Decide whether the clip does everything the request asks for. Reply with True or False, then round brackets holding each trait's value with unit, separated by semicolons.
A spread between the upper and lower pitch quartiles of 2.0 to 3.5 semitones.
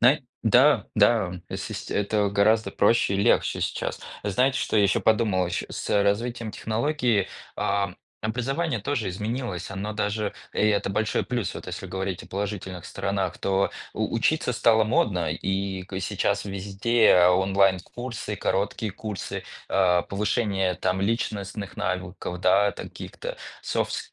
True (3.0 semitones)